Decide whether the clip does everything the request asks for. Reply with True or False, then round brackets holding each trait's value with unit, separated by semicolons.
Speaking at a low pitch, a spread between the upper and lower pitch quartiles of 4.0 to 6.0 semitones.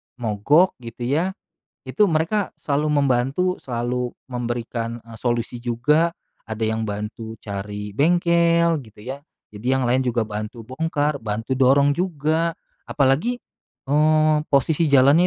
True (130 Hz; 5.2 semitones)